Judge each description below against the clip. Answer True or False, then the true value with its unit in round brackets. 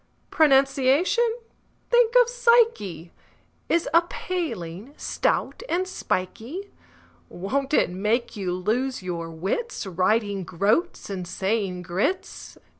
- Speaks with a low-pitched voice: False (230 Hz)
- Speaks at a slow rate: True (100 wpm)